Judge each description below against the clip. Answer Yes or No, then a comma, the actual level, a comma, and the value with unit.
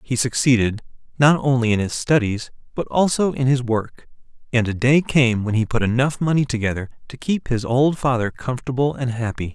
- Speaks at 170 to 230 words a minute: Yes, average, 190 wpm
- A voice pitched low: Yes, low, 125 Hz